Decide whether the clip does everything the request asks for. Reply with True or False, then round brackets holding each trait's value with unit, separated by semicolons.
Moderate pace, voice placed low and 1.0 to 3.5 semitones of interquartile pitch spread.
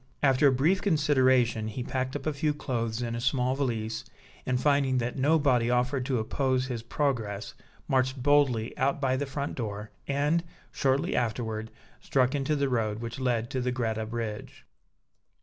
True (165 wpm; 130 Hz; 3.2 semitones)